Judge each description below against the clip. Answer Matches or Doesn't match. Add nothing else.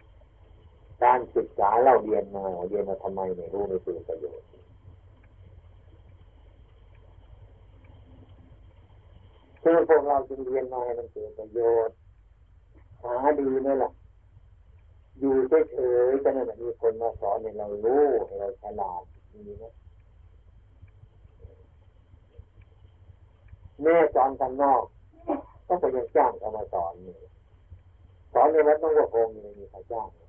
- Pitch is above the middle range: Doesn't match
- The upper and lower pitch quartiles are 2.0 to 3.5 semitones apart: Doesn't match